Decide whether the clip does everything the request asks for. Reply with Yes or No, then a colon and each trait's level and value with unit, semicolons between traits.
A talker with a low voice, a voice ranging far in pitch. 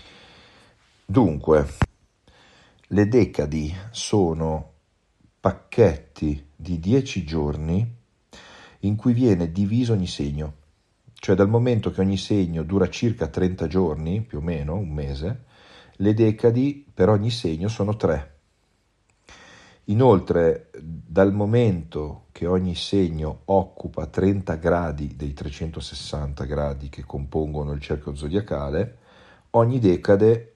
No: very low, 90 Hz; average, 5.0 semitones